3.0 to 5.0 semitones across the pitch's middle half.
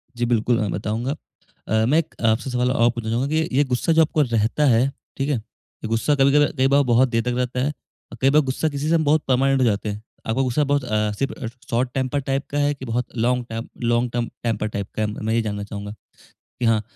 Yes: average, 3.4 semitones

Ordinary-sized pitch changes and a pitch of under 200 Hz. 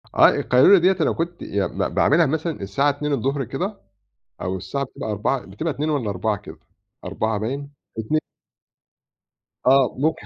No: wide, 6.1 semitones; low, 135 Hz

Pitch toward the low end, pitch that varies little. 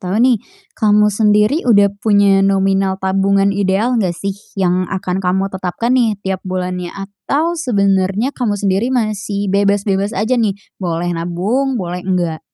No: high, 195 Hz; narrow, 2.0 semitones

